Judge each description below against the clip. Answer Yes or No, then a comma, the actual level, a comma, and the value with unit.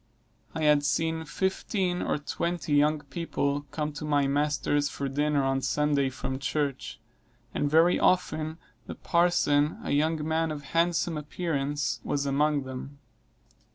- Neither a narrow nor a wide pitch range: No, narrow, 2.2 semitones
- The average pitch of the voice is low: No, medium, 150 Hz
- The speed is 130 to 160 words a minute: Yes, average, 140 wpm